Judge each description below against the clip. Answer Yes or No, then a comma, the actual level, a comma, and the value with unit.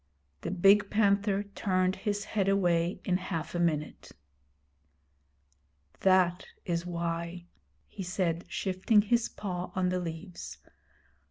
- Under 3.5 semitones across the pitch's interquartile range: Yes, narrow, 2.5 semitones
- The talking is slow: Yes, slow, 115 wpm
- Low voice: No, medium, 185 Hz